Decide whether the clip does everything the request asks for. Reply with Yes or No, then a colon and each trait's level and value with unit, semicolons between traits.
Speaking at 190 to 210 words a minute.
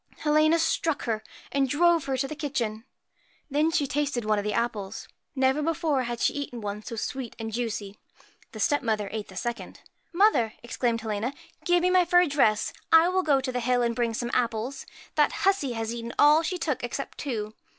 Yes: average, 200 wpm